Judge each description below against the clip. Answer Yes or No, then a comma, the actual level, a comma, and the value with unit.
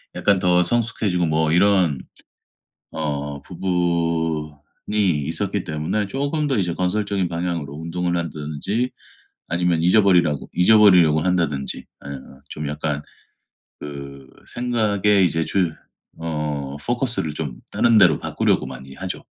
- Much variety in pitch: No, average, 4.6 semitones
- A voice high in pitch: No, very low, 85 Hz